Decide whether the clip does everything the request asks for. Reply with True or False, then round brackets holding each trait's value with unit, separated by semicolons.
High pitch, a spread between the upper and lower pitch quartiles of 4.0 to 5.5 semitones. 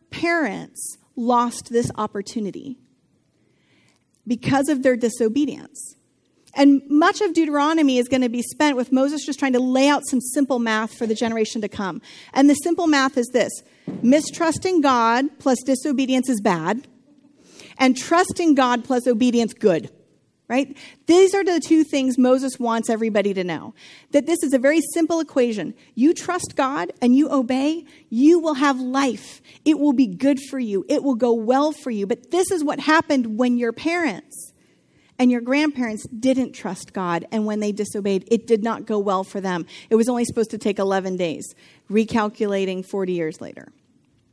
True (255 Hz; 4.3 semitones)